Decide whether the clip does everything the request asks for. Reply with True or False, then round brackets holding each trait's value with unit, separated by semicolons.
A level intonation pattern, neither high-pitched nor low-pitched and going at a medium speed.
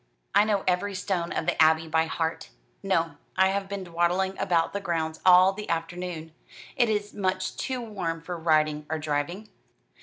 False (3.1 semitones; 175 Hz; 175 wpm)